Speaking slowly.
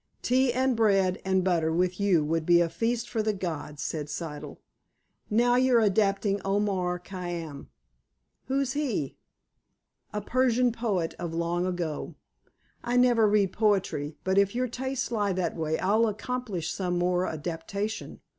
No: average, 145 wpm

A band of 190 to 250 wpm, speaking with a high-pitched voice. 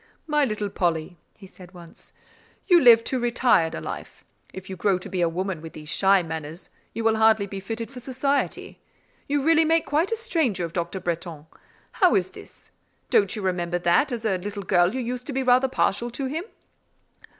Yes: average, 200 wpm; high, 210 Hz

